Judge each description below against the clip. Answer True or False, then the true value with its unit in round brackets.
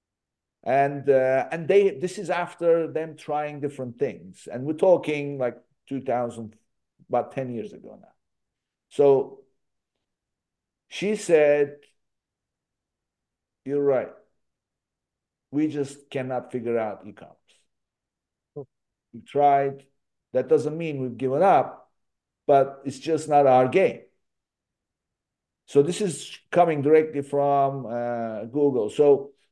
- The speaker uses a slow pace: True (115 wpm)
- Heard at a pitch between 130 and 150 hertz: True (140 Hz)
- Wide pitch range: False (4.2 semitones)